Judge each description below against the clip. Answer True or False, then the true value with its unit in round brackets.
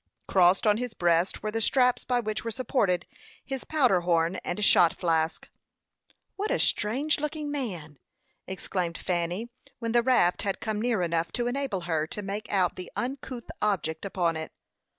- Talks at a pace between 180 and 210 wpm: False (170 wpm)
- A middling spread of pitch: False (5.9 semitones)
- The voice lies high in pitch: True (205 Hz)